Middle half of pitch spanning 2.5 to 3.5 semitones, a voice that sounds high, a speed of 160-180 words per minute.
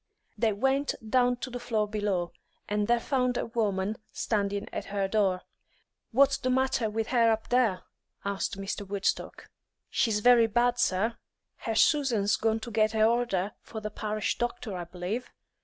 Yes: average, 3.1 semitones; high, 220 Hz; average, 165 wpm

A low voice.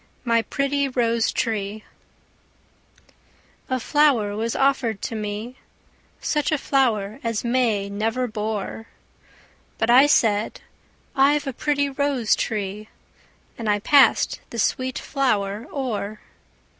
No: high, 230 Hz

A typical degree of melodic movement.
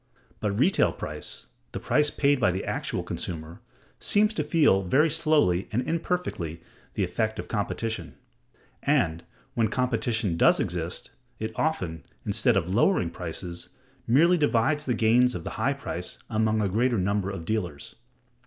No: wide, 7.4 semitones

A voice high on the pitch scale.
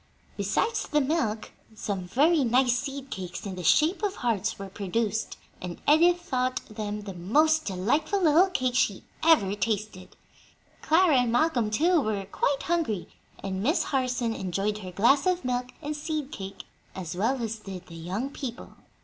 Yes: high, 245 Hz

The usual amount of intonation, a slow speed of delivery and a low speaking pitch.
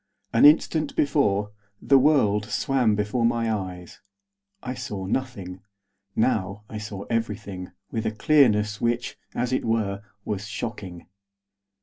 Yes: average, 3.5 semitones; slow, 125 wpm; low, 110 Hz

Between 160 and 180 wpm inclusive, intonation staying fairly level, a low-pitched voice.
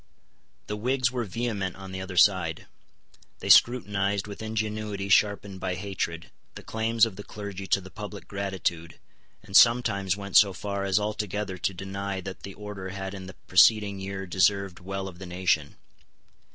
Yes: average, 165 wpm; narrow, 1.8 semitones; low, 100 Hz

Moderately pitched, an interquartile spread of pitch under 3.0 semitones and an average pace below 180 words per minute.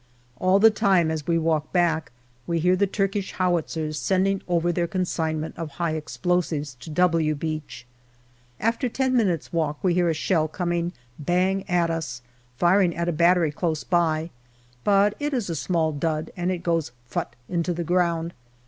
No: medium, 170 Hz; narrow, 2.5 semitones; average, 185 wpm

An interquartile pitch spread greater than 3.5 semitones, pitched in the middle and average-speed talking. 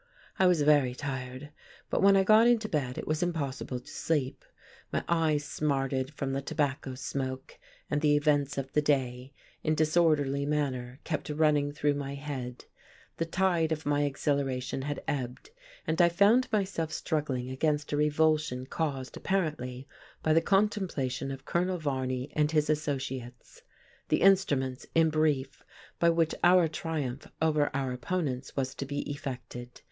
No: average, 3.2 semitones; medium, 145 Hz; average, 155 wpm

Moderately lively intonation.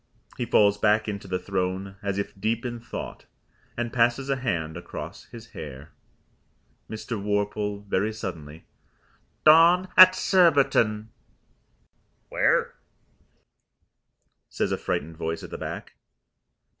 Yes: average, 3.9 semitones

